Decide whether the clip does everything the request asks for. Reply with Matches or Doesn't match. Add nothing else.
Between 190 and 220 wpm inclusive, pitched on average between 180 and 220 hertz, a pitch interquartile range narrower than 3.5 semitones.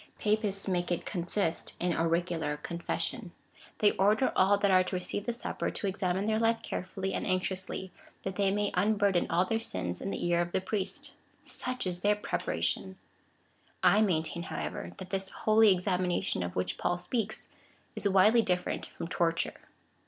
Doesn't match